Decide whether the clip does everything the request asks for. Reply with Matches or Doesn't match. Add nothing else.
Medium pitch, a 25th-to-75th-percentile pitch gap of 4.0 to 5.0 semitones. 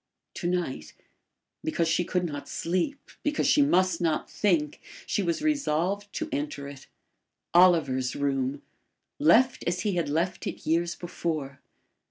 Matches